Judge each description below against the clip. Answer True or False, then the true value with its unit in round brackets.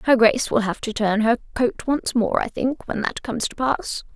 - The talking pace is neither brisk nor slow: False (245 wpm)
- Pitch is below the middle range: False (235 Hz)